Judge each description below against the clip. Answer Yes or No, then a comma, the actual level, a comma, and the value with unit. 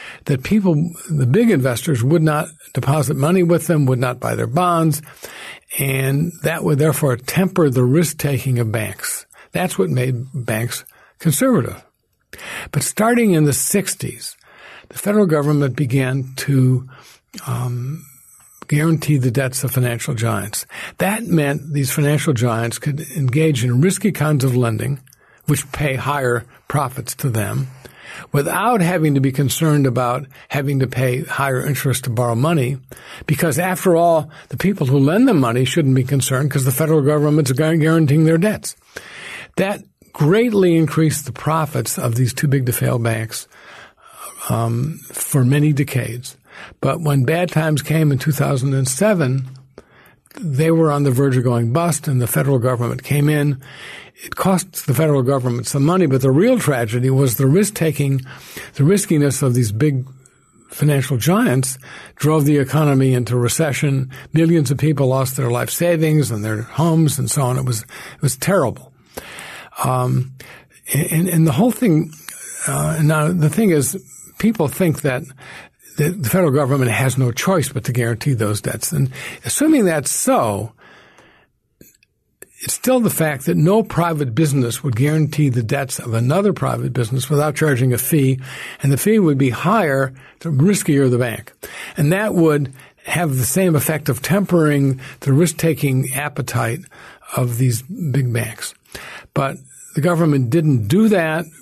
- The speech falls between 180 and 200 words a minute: No, average, 155 wpm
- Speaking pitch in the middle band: Yes, medium, 145 Hz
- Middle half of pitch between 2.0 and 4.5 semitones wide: Yes, average, 3.6 semitones